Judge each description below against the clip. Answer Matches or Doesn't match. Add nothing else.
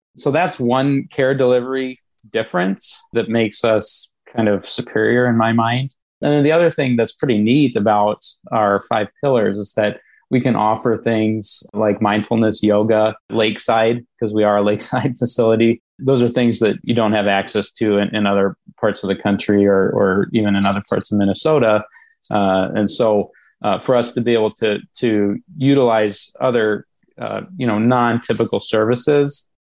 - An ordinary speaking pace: Matches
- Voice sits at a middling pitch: Doesn't match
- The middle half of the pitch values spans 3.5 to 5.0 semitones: Doesn't match